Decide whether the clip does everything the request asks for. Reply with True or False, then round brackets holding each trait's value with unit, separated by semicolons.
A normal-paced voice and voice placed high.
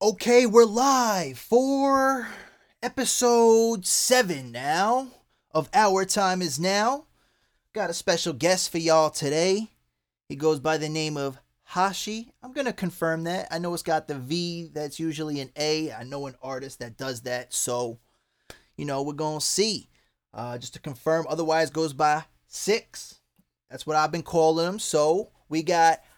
False (160 wpm; 160 Hz)